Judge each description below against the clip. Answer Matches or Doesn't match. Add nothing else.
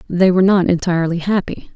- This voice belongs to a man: Doesn't match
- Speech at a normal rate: Matches